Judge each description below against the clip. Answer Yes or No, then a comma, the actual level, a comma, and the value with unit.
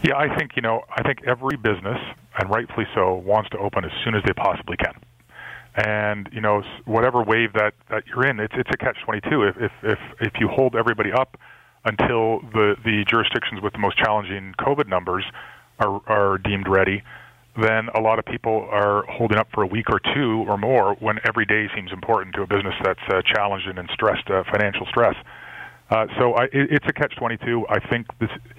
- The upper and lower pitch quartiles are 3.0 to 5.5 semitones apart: No, narrow, 2.6 semitones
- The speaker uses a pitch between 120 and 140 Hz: No, low, 110 Hz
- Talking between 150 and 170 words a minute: No, average, 200 wpm